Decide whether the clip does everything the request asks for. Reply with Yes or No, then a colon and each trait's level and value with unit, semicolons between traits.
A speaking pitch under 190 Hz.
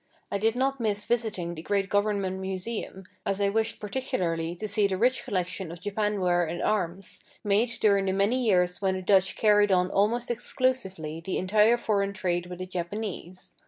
No: high, 200 Hz